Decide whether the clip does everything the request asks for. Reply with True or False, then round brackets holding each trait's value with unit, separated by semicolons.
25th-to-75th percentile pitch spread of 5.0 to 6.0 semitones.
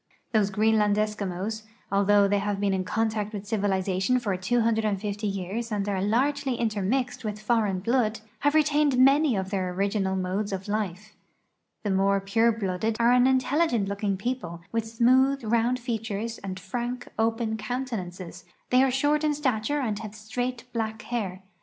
False (3.5 semitones)